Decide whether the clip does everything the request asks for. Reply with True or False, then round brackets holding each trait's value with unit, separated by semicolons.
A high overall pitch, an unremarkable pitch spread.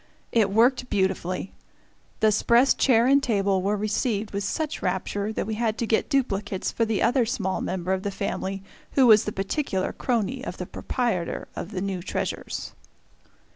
True (210 Hz; 3.6 semitones)